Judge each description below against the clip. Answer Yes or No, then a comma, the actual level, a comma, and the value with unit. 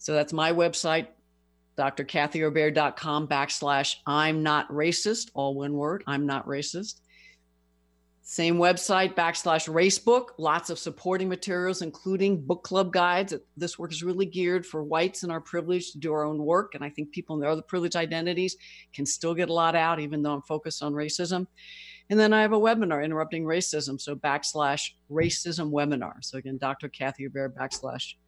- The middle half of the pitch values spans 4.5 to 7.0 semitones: No, average, 3.5 semitones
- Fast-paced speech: No, average, 165 wpm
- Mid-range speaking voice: Yes, medium, 160 Hz